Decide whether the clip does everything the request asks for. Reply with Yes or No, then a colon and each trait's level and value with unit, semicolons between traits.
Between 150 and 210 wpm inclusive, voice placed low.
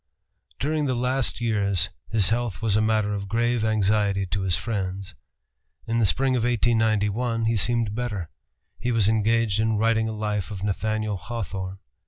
Yes: average, 165 wpm; low, 110 Hz